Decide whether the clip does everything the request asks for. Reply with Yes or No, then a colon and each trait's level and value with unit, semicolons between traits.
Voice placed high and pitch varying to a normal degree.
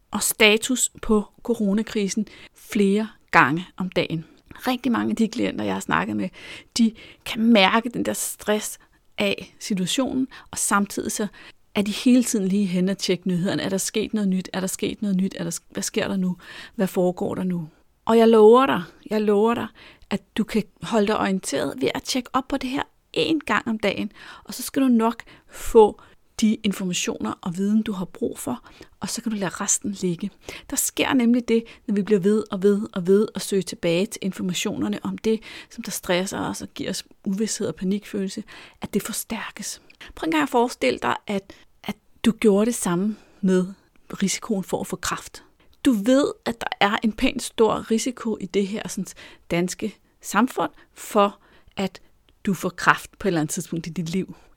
Yes: high, 205 Hz; average, 3.2 semitones